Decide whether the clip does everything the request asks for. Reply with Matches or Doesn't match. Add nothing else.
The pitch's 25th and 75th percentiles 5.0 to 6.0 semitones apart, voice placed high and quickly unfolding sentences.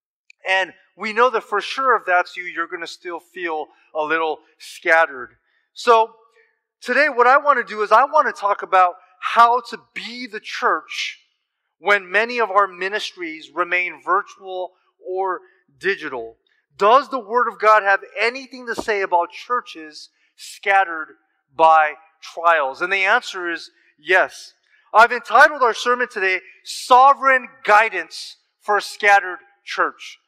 Doesn't match